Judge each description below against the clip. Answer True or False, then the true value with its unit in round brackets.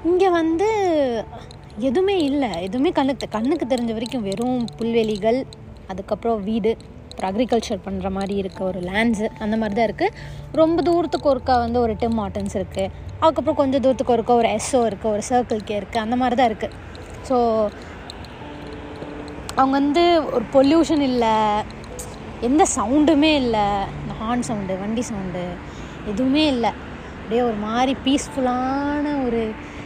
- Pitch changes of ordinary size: True (4.4 semitones)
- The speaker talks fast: True (135 wpm)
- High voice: True (240 Hz)